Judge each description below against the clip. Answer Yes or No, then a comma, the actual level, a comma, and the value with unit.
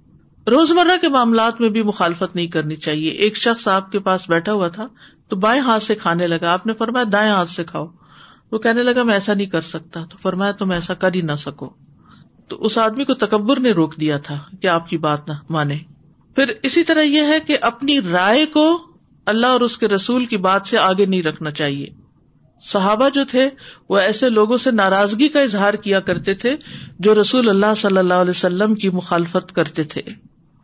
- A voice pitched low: No, high, 200 Hz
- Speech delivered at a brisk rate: Yes, fast, 210 wpm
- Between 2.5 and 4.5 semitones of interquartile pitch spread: No, wide, 5.4 semitones